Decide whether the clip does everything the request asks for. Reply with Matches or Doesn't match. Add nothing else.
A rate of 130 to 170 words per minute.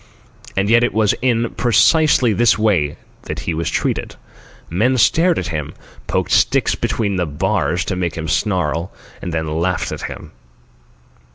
Matches